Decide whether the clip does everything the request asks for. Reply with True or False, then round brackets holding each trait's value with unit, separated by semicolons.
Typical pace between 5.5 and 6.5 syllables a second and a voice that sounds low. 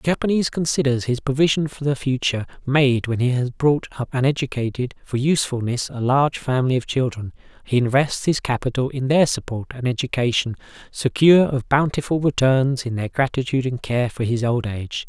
True (5.8 syllables/s; 130 Hz)